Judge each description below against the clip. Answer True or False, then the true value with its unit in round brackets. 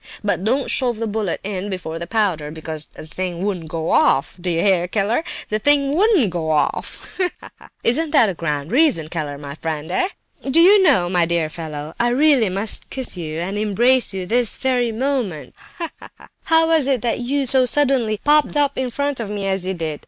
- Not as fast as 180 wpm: False (205 wpm)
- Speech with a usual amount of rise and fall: False (7.7 semitones)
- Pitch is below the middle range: False (210 Hz)